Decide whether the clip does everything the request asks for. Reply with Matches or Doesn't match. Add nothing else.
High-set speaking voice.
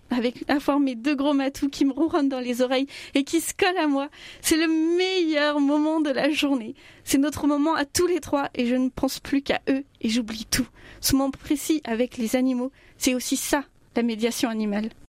Matches